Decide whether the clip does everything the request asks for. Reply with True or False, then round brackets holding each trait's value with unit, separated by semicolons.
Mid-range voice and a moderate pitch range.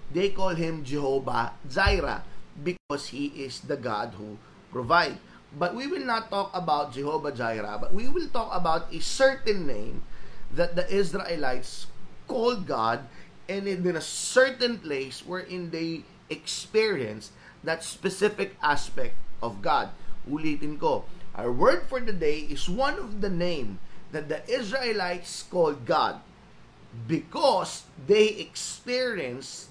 False (175 Hz; 6.2 semitones)